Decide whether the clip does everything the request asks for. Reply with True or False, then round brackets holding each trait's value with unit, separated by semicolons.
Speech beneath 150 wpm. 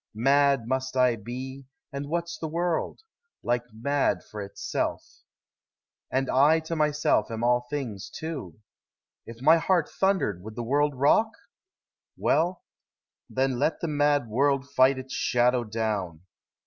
True (140 wpm)